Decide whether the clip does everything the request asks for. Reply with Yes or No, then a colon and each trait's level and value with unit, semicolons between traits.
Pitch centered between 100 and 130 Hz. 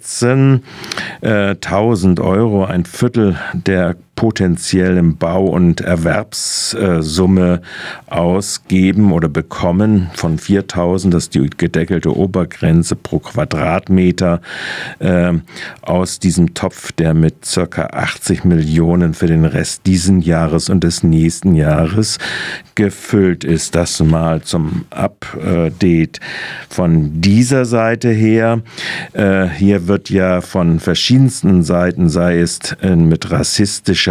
No: very low, 90 Hz